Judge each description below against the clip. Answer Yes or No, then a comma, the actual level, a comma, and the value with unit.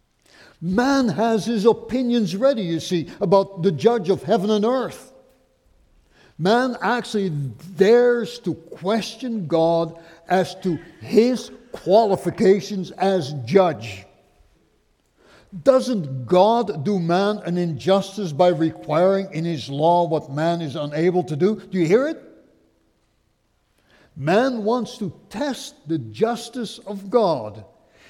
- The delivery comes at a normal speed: No, slow, 115 wpm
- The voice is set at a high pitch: Yes, high, 195 Hz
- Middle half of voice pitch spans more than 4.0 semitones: Yes, average, 5.3 semitones